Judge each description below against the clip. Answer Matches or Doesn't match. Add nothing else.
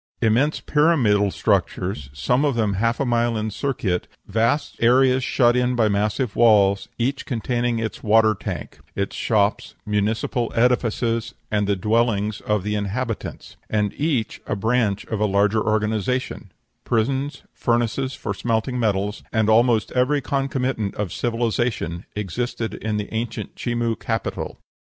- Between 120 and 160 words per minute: Matches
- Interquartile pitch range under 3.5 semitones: Matches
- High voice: Doesn't match